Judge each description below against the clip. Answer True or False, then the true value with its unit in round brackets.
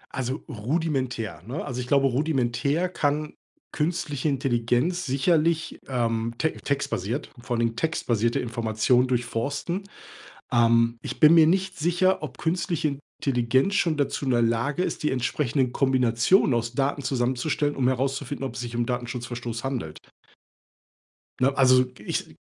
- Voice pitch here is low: True (130 Hz)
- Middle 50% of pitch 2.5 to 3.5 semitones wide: False (4.1 semitones)